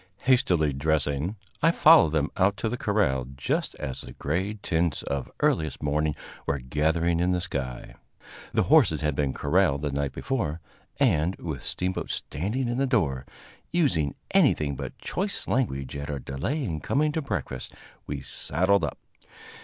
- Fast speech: No, average, 160 wpm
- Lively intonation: Yes, wide, 6.6 semitones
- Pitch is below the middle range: Yes, very low, 80 Hz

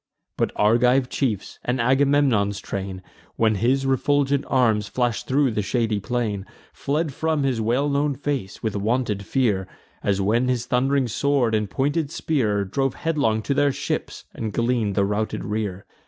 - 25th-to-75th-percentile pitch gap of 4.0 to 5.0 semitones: Yes, average, 4.5 semitones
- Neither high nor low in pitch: No, low, 120 Hz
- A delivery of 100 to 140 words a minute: No, average, 155 wpm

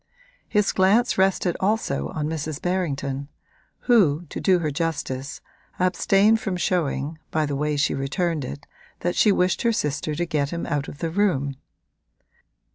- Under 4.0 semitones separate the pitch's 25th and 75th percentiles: No, average, 4.6 semitones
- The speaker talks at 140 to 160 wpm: Yes, average, 155 wpm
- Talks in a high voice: No, medium, 165 Hz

